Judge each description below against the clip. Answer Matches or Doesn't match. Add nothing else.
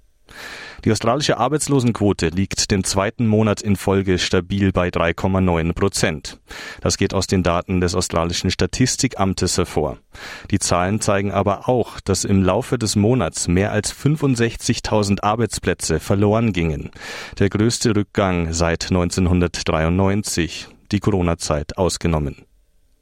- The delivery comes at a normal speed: Doesn't match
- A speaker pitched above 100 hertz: Doesn't match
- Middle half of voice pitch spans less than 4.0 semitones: Matches